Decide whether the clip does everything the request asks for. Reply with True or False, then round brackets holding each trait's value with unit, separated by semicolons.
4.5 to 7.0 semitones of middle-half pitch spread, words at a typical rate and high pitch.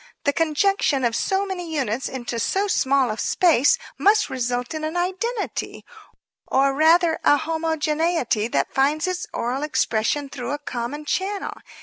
True (5.1 semitones; 150 wpm; 300 Hz)